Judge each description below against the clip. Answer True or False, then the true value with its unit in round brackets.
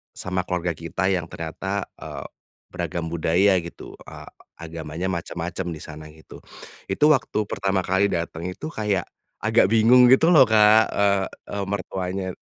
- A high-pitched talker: False (95 Hz)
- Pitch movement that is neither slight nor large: True (3.3 semitones)